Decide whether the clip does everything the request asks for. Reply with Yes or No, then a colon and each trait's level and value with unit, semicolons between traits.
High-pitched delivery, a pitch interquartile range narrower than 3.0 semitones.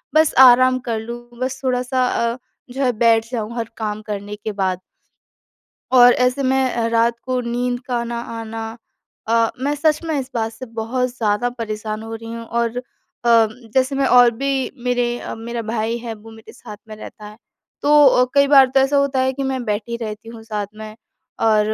Yes: high, 235 Hz; narrow, 2.5 semitones